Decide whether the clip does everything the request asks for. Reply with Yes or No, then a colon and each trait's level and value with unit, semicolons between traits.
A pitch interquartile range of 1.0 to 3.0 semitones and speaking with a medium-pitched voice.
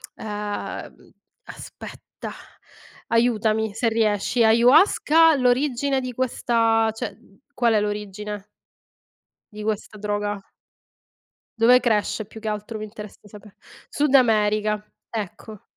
No: narrow, 2.5 semitones; high, 220 Hz